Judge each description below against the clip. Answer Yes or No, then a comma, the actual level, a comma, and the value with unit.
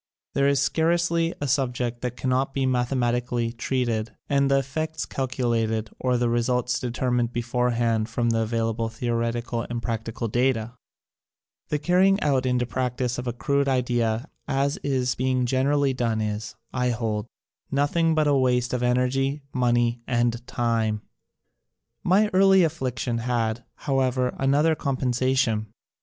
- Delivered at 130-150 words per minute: Yes, average, 140 wpm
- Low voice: Yes, low, 125 Hz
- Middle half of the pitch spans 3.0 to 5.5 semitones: No, narrow, 2.5 semitones